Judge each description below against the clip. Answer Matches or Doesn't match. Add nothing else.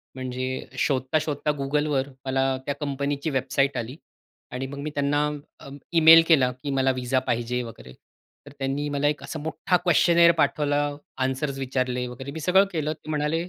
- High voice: Doesn't match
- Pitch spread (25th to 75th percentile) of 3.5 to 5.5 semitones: Doesn't match